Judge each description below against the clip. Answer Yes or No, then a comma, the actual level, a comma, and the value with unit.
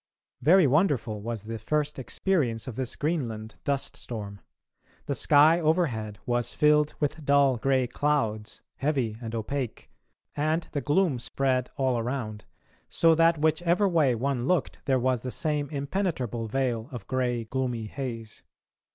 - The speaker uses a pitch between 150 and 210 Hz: No, low, 130 Hz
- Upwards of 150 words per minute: No, average, 145 wpm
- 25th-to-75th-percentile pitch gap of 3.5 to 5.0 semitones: Yes, average, 4.4 semitones